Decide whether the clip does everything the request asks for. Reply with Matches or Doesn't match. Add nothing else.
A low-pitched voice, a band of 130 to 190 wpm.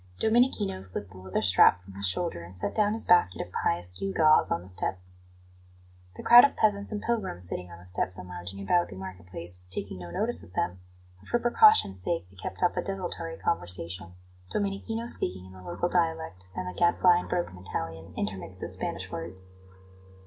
Doesn't match